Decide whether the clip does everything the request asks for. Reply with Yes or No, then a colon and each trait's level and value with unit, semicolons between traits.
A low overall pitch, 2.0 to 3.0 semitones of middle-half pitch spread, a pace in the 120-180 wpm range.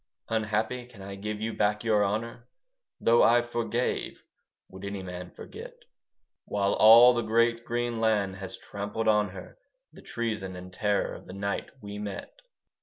Yes: low, 105 Hz; average, 2.7 semitones; average, 160 wpm